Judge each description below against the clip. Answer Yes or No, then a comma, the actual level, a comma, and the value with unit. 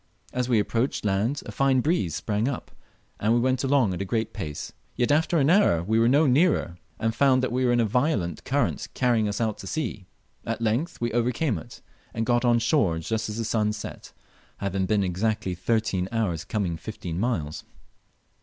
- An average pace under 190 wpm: No, average, 195 wpm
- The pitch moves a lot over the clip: No, average, 4.4 semitones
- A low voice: Yes, low, 115 Hz